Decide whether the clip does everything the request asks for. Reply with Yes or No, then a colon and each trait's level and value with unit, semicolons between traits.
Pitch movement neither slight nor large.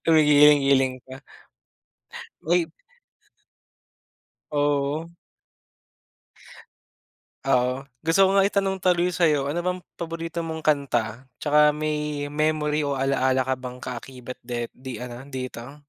Yes: average, 3.5 semitones